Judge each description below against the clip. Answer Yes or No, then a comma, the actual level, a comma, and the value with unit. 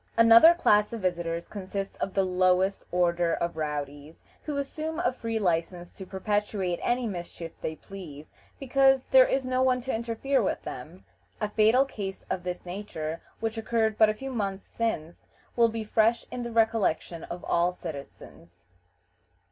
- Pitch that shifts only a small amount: No, average, 4.9 semitones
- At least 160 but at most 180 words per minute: Yes, average, 165 wpm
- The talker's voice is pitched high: Yes, high, 205 Hz